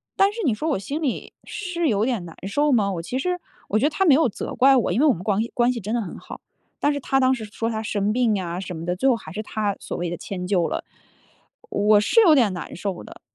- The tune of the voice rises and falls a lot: Yes, wide, 5.8 semitones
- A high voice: Yes, high, 220 Hz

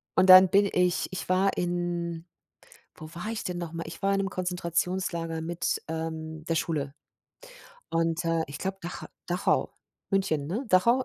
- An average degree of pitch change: No, narrow, 2.2 semitones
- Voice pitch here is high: No, medium, 175 Hz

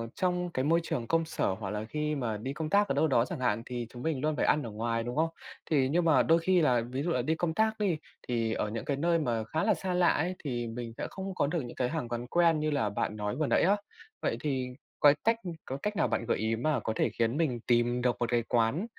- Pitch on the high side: No, medium, 140 Hz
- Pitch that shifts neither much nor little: No, wide, 5.7 semitones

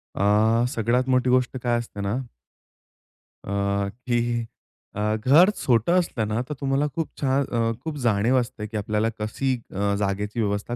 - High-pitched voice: No, low, 115 Hz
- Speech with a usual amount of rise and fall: Yes, average, 3.5 semitones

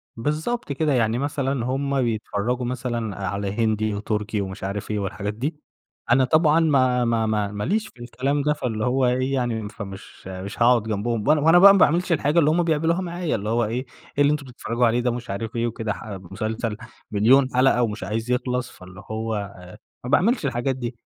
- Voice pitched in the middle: No, low, 120 Hz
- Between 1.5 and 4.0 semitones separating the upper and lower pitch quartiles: No, average, 4.4 semitones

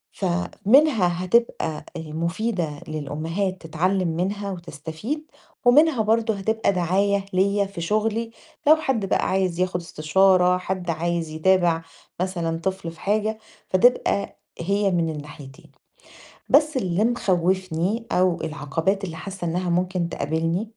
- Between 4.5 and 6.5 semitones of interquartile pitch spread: No, average, 3.7 semitones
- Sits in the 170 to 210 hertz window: Yes, medium, 185 Hz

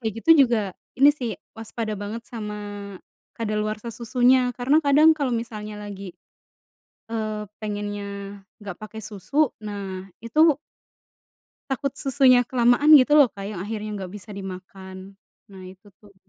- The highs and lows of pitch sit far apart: No, average, 3.6 semitones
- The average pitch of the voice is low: No, high, 215 Hz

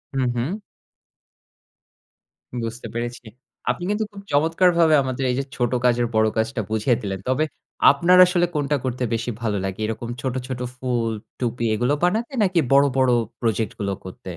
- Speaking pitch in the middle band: No, low, 125 Hz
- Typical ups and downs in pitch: Yes, average, 4.8 semitones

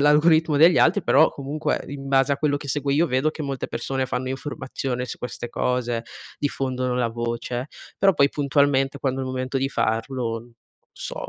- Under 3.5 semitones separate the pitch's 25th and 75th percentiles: Yes, narrow, 2.4 semitones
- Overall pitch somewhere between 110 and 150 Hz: Yes, low, 135 Hz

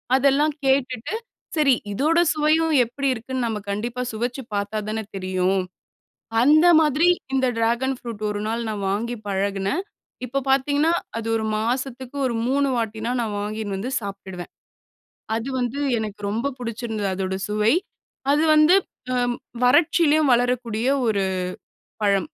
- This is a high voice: Yes, high, 240 Hz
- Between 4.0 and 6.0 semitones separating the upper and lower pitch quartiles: Yes, average, 4.4 semitones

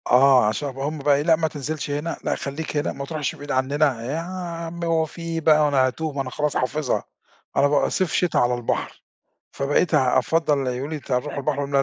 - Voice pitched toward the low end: No, medium, 145 Hz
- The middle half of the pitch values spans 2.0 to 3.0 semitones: Yes, average, 2.7 semitones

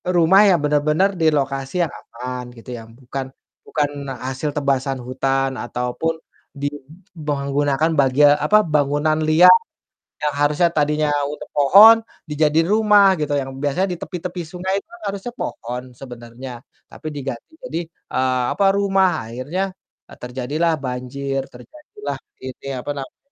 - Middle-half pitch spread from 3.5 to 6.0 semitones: Yes, average, 4.1 semitones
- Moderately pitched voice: Yes, medium, 145 Hz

